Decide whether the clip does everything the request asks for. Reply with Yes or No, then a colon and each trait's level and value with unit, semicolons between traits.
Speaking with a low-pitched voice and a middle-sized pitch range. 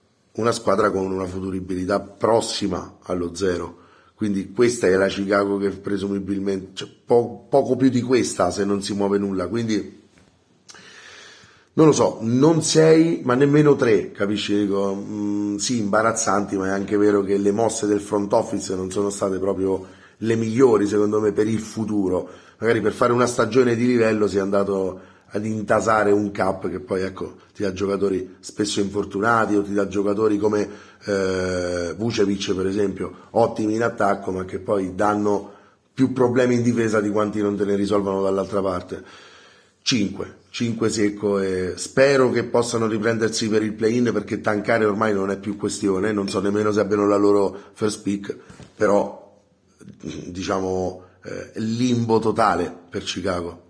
No: low, 100 Hz; narrow, 2.2 semitones